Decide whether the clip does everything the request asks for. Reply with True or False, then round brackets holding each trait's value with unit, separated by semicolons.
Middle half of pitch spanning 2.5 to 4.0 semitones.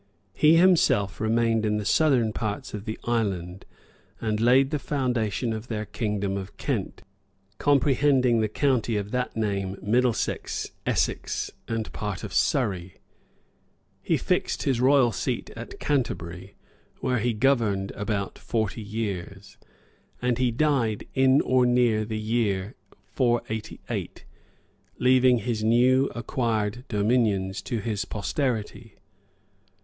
True (3.4 semitones)